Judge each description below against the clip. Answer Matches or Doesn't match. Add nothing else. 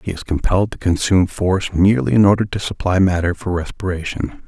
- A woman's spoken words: Doesn't match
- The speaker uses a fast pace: Doesn't match